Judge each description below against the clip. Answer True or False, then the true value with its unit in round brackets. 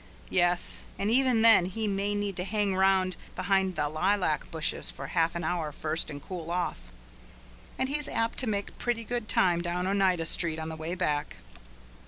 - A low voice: False (185 Hz)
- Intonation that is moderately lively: True (3.8 semitones)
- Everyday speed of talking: True (185 wpm)